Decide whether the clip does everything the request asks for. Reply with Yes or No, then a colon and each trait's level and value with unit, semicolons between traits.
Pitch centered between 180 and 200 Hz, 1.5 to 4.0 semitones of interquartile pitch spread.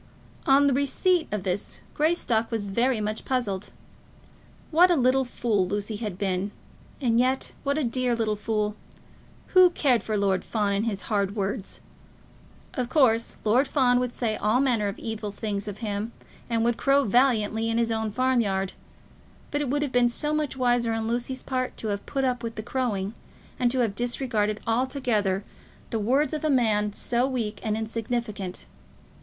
No: high, 230 Hz; average, 3.6 semitones